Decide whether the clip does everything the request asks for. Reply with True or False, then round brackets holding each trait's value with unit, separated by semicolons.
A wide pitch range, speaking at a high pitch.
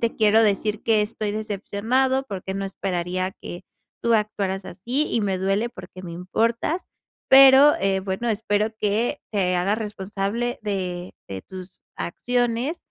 False (3.4 semitones; 205 Hz)